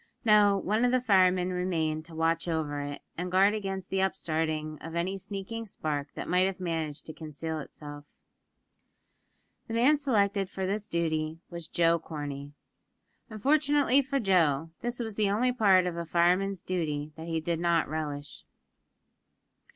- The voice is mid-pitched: Yes, medium, 180 Hz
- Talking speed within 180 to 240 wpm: No, average, 160 wpm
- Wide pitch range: No, average, 4.1 semitones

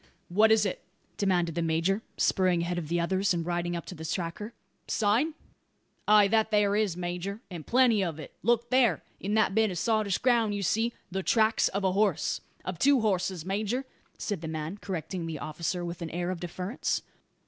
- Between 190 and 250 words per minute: Yes, average, 200 wpm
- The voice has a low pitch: No, high, 190 Hz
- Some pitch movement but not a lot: Yes, average, 3.8 semitones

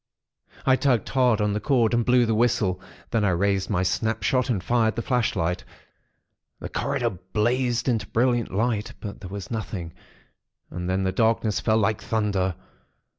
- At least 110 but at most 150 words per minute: No, average, 165 wpm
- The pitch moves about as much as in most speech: Yes, average, 3.5 semitones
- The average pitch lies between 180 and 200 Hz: No, low, 110 Hz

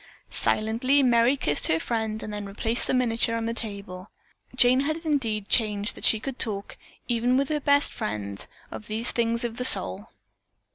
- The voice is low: No, high, 230 Hz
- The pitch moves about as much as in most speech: Yes, average, 3.2 semitones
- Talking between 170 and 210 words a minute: Yes, average, 180 wpm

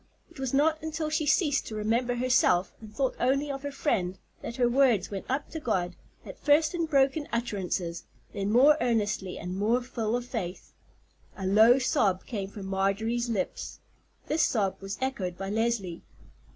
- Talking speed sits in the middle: Yes, average, 175 wpm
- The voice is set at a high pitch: Yes, high, 235 Hz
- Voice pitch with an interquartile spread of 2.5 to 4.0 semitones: No, wide, 5.6 semitones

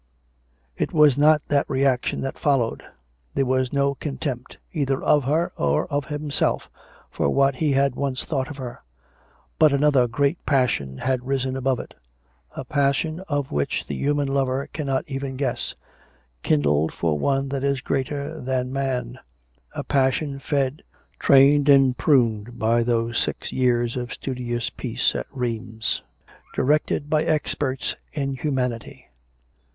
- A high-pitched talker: No, low, 135 Hz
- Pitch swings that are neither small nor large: No, narrow, 2.3 semitones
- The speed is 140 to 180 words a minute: Yes, average, 145 wpm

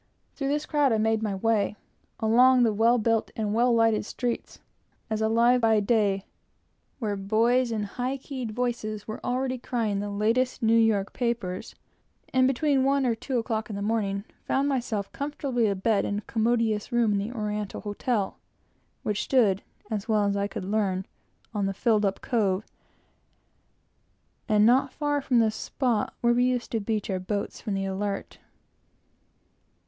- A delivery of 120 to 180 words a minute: Yes, average, 170 wpm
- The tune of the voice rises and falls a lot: No, average, 3.1 semitones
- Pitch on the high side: Yes, high, 225 Hz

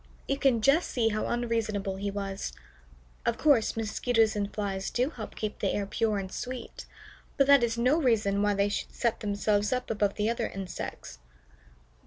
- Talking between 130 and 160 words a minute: No, average, 180 wpm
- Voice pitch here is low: No, high, 215 Hz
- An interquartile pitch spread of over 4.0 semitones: No, average, 3.0 semitones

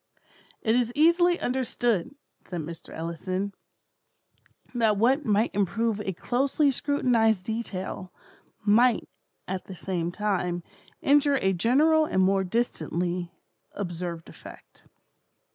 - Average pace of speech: No, slow, 110 wpm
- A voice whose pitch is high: Yes, high, 210 Hz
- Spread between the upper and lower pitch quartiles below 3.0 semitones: No, wide, 5.4 semitones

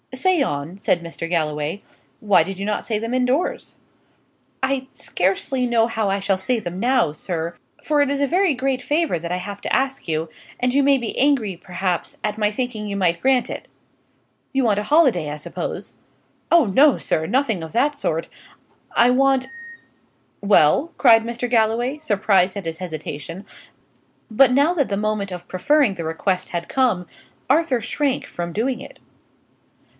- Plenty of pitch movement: Yes, wide, 6.5 semitones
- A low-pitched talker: No, high, 220 Hz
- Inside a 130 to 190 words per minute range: Yes, average, 175 wpm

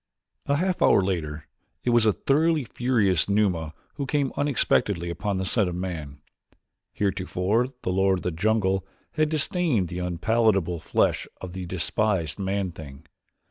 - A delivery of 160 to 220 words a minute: No, average, 150 wpm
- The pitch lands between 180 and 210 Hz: No, very low, 95 Hz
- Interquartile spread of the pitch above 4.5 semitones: Yes, average, 5.1 semitones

